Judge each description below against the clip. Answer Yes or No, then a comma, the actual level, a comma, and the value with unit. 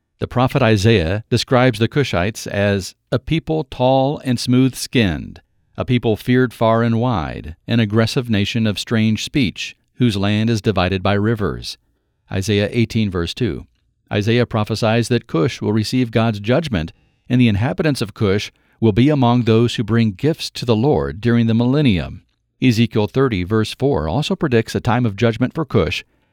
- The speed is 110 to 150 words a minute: No, average, 165 wpm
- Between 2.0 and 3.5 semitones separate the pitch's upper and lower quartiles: Yes, average, 3.1 semitones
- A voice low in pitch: Yes, low, 115 Hz